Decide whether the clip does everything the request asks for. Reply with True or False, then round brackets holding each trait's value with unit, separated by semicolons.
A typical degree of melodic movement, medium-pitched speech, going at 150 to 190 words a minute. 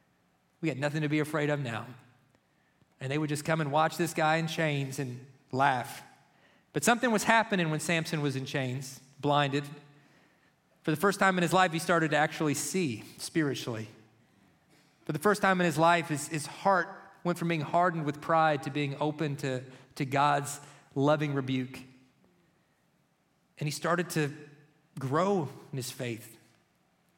True (3.1 semitones; 150 Hz; 170 wpm)